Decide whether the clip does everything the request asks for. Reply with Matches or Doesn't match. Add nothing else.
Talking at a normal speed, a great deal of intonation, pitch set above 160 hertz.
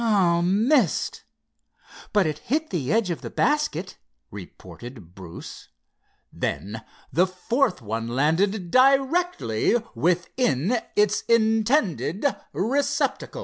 Doesn't match